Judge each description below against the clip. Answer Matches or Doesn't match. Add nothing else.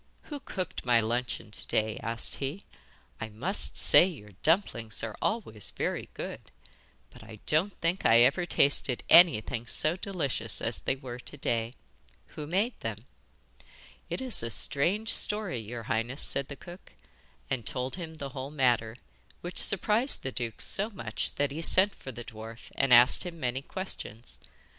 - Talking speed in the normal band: Matches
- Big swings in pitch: Matches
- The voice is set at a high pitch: Doesn't match